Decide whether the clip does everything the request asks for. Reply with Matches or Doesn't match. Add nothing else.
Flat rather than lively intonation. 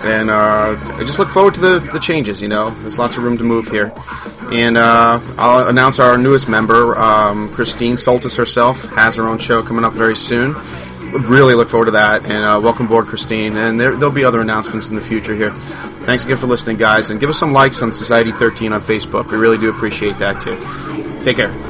Matches